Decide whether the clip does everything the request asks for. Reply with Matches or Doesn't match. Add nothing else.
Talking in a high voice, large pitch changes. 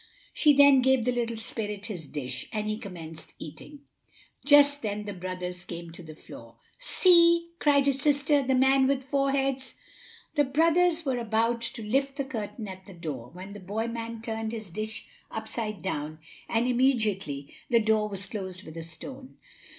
Matches